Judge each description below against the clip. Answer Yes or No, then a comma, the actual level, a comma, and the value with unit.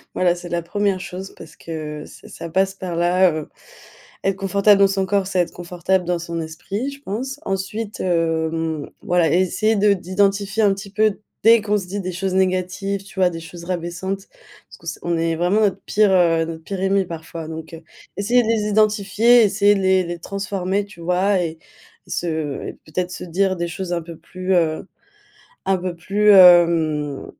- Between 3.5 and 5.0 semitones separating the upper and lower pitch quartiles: No, average, 2.7 semitones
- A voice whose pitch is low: No, medium, 185 Hz